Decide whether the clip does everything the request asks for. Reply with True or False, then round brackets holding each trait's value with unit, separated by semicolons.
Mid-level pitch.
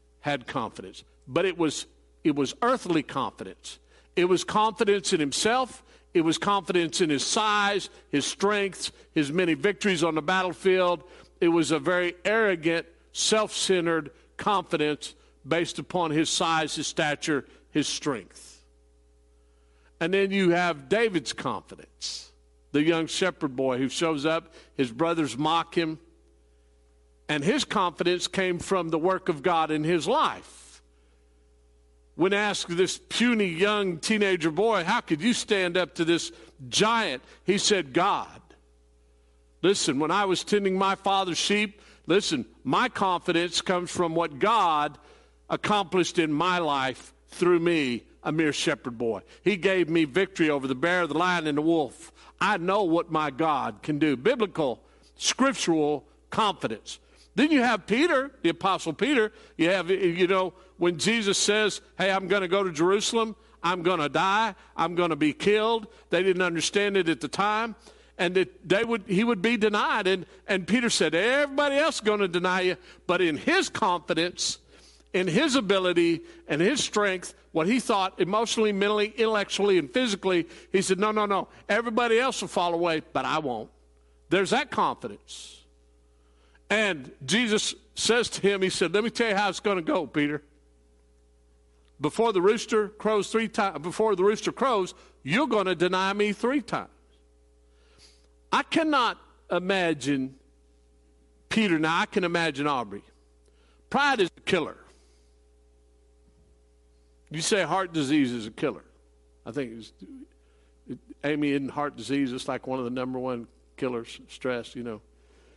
True (170 Hz)